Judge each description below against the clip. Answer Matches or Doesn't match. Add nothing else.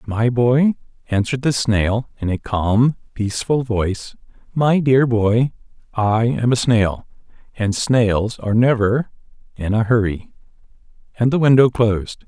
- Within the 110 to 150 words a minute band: Matches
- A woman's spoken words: Doesn't match